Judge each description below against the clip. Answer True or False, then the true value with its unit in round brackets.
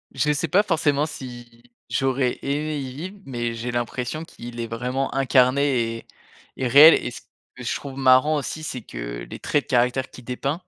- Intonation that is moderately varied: True (3.2 semitones)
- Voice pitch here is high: False (130 Hz)